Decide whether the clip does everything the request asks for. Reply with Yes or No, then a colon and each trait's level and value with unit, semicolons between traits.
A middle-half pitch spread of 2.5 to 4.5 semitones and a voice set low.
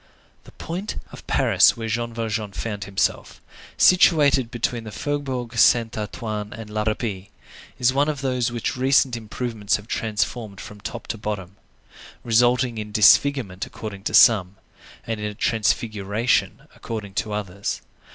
Yes: average, 2.8 semitones; low, 115 Hz